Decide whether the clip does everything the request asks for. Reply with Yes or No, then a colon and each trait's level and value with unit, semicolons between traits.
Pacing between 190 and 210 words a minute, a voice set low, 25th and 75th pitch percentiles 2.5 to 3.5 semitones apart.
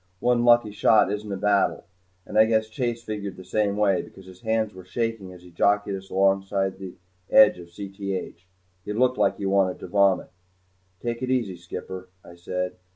Yes: average, 195 wpm; low, 100 Hz; average, 2.8 semitones